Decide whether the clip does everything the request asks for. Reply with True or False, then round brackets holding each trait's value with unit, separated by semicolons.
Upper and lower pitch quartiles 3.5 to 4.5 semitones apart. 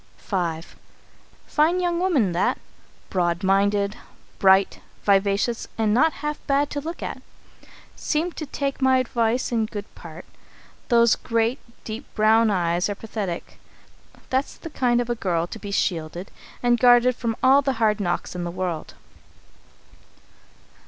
False (5.3 semitones)